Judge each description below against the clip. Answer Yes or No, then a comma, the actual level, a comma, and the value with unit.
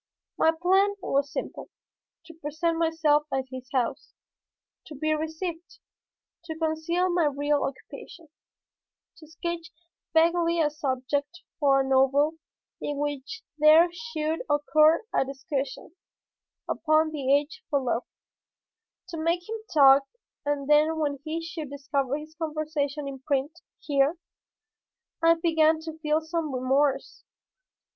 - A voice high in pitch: Yes, very high, 310 Hz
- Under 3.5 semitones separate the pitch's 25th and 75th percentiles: Yes, narrow, 2.5 semitones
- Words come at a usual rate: No, slow, 125 wpm